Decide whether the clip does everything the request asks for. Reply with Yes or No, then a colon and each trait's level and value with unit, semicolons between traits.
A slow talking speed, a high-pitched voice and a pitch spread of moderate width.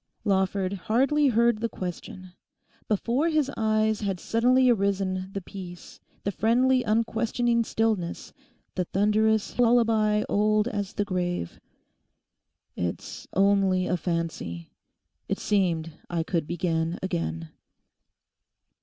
Yes: slow, 110 wpm; high, 200 Hz; average, 3.8 semitones